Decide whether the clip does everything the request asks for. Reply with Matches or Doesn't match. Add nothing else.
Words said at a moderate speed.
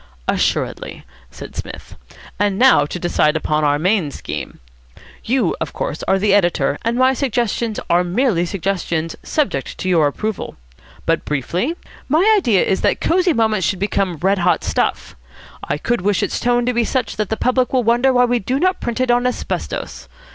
Matches